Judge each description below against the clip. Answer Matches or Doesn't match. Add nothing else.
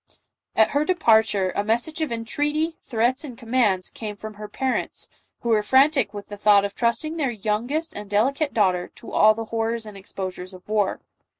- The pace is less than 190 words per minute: Doesn't match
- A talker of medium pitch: Doesn't match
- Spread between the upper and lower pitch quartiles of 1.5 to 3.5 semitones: Doesn't match